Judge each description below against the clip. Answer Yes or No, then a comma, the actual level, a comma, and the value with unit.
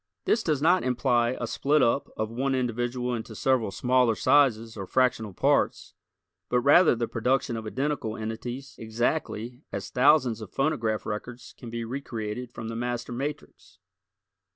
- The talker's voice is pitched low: Yes, low, 120 Hz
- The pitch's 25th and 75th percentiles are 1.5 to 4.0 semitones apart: Yes, average, 2.8 semitones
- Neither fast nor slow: Yes, average, 155 wpm